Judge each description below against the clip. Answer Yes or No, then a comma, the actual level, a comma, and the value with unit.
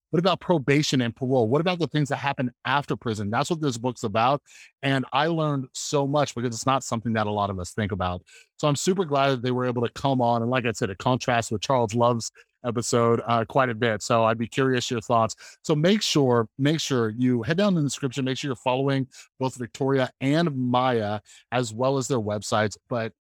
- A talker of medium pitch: No, low, 125 Hz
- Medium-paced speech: No, fast, 230 wpm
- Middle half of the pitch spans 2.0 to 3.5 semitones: Yes, average, 3.2 semitones